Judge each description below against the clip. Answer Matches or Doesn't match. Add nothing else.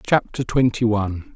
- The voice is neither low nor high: Doesn't match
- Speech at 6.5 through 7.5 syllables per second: Doesn't match